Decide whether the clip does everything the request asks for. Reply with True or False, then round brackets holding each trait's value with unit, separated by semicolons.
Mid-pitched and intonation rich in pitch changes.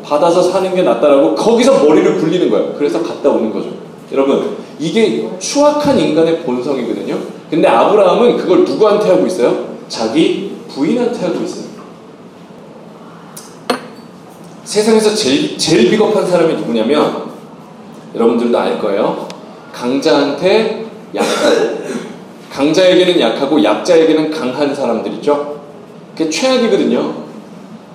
False (200 Hz; 5.9 semitones)